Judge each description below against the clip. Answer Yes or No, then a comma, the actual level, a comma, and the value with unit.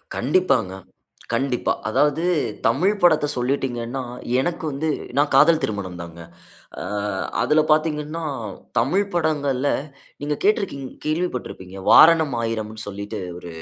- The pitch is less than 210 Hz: Yes, medium, 140 Hz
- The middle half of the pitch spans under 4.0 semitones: No, wide, 5.6 semitones